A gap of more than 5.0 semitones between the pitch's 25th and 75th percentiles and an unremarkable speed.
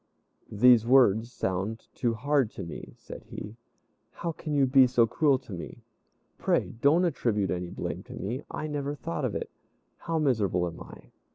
Yes: wide, 5.6 semitones; average, 175 wpm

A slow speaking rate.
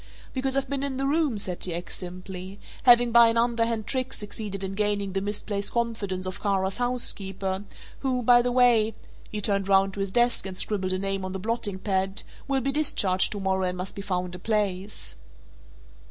No: average, 195 wpm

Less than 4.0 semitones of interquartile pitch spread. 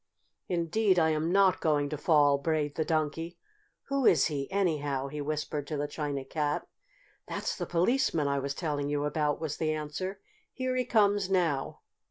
Yes: average, 3.6 semitones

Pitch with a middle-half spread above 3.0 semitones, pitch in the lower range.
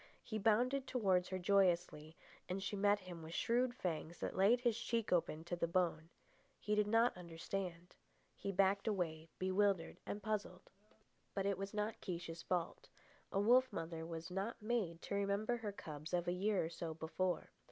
No: average, 3.7 semitones; high, 190 Hz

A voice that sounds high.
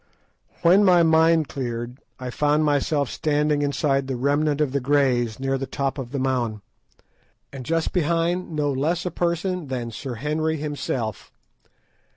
No: medium, 145 Hz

